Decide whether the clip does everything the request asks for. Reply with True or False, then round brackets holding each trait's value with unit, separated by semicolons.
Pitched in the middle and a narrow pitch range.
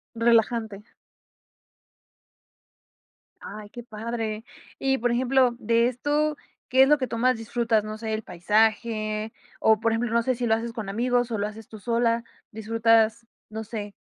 False (230 Hz; 1.8 semitones)